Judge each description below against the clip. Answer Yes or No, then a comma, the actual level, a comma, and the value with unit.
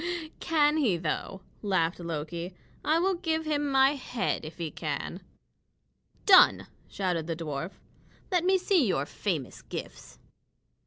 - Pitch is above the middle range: Yes, high, 195 Hz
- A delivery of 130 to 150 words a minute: Yes, slow, 135 wpm